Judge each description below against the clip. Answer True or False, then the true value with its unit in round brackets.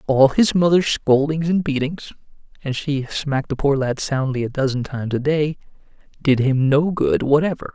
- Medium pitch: True (145 Hz)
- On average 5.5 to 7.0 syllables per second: False (5.0 syllables/s)